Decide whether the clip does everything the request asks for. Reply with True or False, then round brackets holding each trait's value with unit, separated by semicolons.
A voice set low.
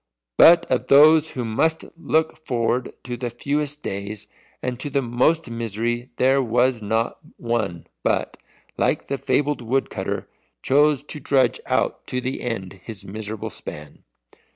True (125 Hz)